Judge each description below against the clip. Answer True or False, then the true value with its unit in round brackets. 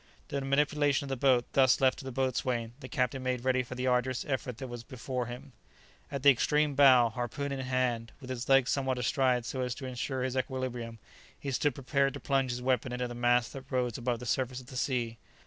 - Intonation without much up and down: True (1.6 semitones)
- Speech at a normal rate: False (225 wpm)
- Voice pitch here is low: True (130 Hz)